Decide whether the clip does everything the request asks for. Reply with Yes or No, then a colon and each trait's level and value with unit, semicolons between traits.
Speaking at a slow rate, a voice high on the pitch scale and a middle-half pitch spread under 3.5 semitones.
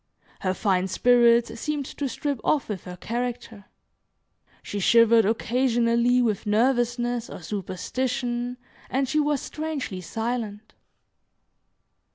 Yes: slow, 110 wpm; high, 235 Hz; average, 2.8 semitones